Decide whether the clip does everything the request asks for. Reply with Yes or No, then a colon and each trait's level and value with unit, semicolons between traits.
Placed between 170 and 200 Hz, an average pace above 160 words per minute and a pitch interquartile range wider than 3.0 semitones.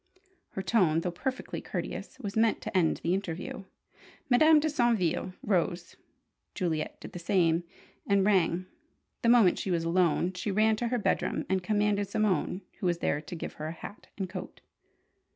Yes: high, 190 Hz; average, 170 wpm; average, 3.8 semitones